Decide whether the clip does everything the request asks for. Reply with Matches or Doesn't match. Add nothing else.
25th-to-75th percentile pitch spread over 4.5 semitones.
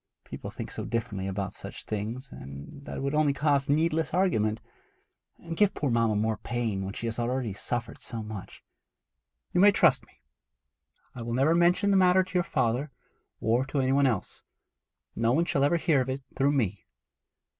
Matches